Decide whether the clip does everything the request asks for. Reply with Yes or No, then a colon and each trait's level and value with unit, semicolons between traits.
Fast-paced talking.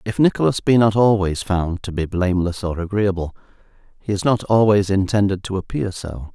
No: average, 180 wpm